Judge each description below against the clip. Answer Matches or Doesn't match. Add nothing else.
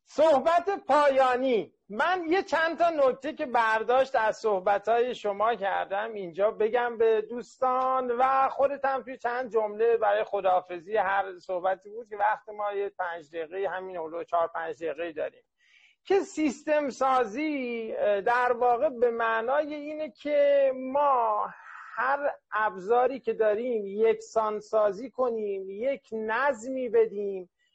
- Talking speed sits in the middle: Matches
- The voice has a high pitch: Matches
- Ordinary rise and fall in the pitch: Matches